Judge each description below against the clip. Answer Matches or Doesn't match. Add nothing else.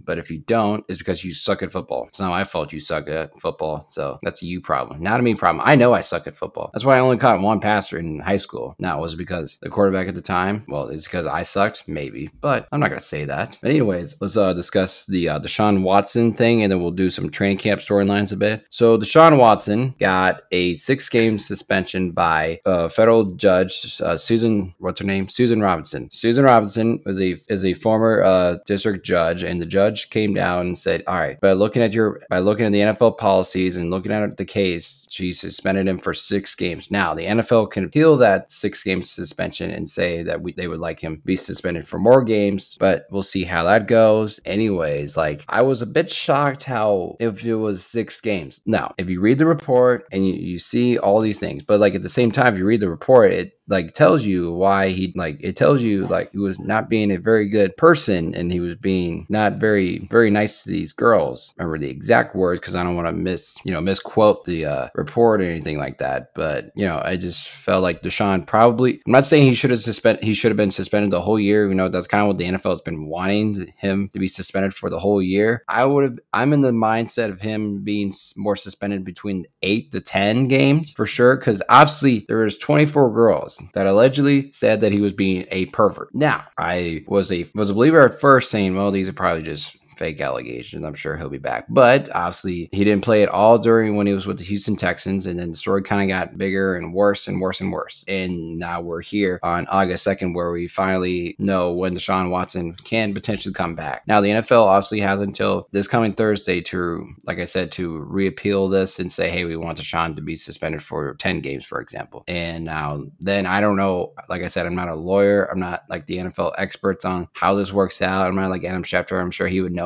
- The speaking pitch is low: Matches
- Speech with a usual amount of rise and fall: Matches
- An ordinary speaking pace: Doesn't match